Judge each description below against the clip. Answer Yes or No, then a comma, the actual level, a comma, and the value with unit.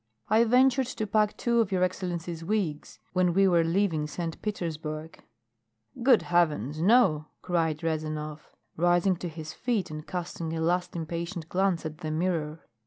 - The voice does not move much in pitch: No, average, 3.5 semitones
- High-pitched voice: No, medium, 170 Hz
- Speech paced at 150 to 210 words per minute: Yes, average, 160 wpm